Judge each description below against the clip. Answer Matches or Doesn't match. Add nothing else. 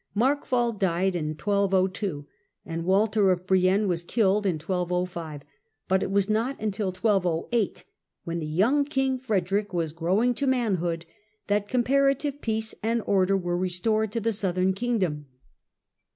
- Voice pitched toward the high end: Matches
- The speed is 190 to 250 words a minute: Doesn't match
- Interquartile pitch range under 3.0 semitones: Doesn't match